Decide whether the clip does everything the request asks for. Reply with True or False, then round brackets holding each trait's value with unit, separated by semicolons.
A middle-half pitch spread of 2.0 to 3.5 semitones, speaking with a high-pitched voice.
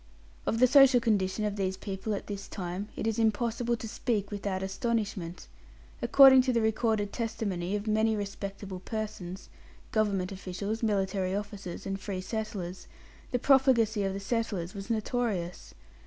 True (2.8 semitones; 205 Hz)